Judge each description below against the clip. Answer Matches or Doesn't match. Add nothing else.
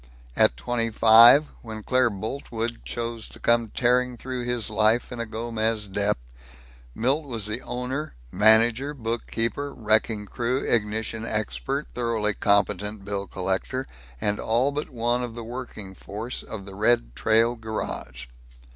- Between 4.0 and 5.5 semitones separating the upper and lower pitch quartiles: Doesn't match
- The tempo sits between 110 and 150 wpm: Matches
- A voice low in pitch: Matches